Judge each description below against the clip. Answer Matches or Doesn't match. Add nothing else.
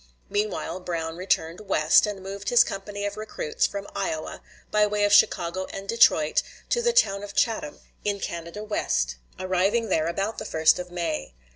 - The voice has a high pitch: Matches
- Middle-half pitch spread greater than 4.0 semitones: Doesn't match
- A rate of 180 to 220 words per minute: Doesn't match